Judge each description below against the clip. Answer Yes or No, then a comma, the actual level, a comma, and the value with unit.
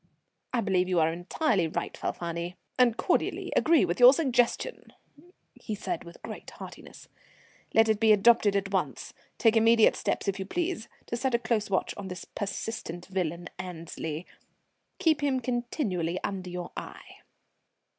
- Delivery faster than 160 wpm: No, average, 155 wpm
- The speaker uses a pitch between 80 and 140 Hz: No, high, 200 Hz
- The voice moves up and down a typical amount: Yes, average, 5.0 semitones